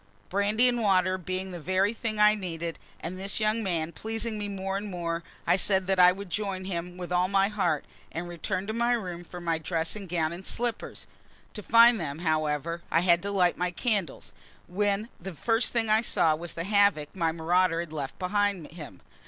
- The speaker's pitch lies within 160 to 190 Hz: Yes, medium, 185 Hz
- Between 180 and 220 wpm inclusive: Yes, average, 200 wpm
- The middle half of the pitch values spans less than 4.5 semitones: Yes, average, 3.4 semitones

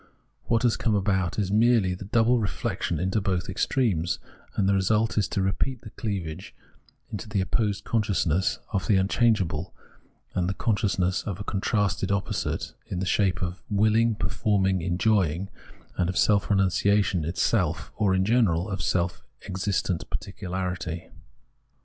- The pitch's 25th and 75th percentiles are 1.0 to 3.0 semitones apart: Yes, narrow, 2.6 semitones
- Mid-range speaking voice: No, very low, 95 Hz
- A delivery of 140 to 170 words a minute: Yes, average, 150 wpm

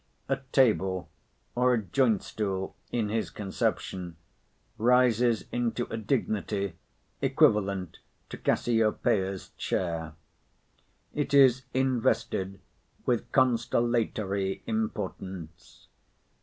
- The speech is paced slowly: Yes, slow, 85 wpm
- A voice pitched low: Yes, low, 110 Hz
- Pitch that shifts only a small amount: No, average, 4.1 semitones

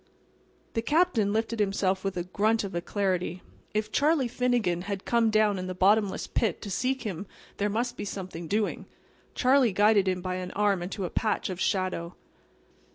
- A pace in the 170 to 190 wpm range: Yes, average, 175 wpm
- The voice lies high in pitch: Yes, high, 205 Hz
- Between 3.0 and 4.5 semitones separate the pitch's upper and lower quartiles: Yes, average, 3.3 semitones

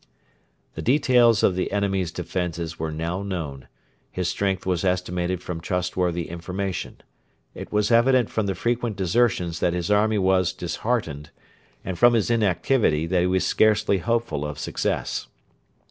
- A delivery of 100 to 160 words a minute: Yes, average, 145 wpm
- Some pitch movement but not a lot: Yes, average, 3.8 semitones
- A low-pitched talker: Yes, very low, 95 Hz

